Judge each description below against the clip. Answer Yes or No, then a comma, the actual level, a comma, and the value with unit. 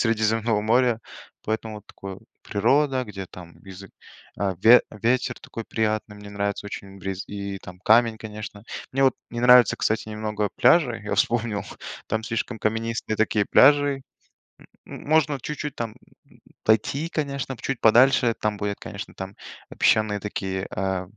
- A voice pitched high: No, low, 110 Hz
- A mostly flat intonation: No, average, 3.0 semitones